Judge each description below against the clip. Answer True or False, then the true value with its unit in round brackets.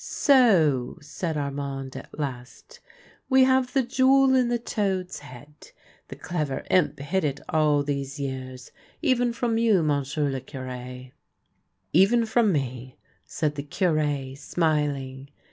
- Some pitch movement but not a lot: False (8.1 semitones)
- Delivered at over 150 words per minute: False (145 wpm)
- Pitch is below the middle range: False (150 Hz)